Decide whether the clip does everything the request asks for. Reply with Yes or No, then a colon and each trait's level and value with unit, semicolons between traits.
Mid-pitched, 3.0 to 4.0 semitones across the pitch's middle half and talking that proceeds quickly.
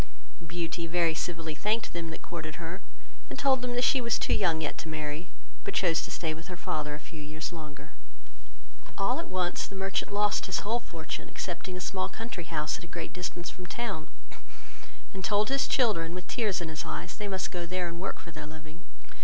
Yes: medium, 175 Hz; average, 3.5 semitones; fast, 210 wpm